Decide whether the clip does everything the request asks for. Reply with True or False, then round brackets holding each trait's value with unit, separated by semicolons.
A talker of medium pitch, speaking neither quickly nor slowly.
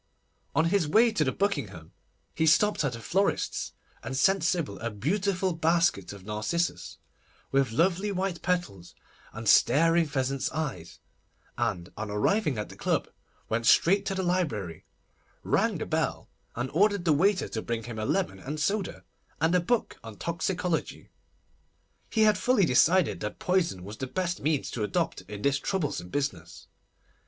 True (155 Hz; 160 wpm)